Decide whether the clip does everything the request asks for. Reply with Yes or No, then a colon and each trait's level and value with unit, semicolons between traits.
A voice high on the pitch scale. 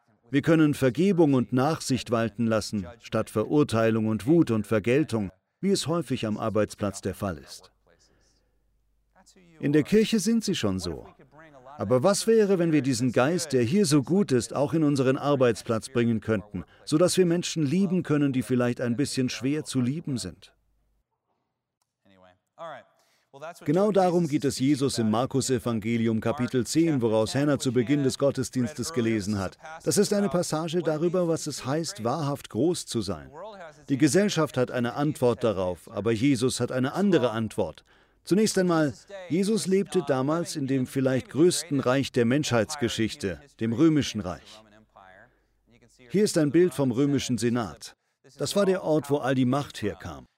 No: low, 130 Hz